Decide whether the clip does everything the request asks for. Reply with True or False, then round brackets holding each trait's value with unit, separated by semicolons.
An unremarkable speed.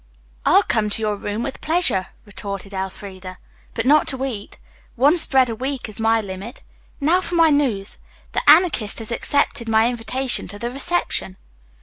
True (165 wpm)